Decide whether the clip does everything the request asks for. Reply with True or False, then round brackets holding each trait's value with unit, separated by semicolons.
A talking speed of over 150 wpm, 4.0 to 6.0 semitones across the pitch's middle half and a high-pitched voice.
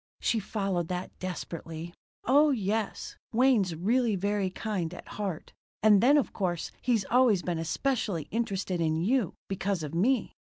False (145 wpm; 4.7 semitones; 195 Hz)